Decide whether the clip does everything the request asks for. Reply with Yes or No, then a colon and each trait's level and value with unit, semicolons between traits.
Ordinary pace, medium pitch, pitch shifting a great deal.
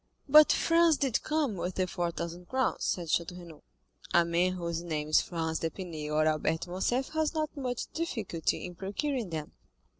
Yes: average, 180 wpm; medium, 180 Hz; wide, 7.8 semitones